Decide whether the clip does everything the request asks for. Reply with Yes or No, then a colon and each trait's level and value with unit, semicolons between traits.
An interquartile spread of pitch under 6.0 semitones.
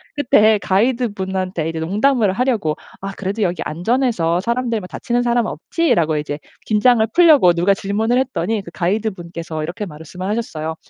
Yes: wide, 5.5 semitones